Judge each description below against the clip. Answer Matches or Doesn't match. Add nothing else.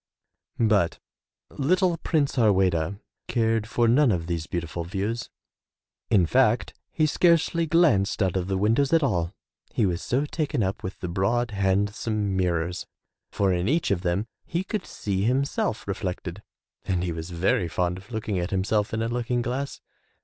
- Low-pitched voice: Matches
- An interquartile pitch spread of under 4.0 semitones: Doesn't match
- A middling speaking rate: Matches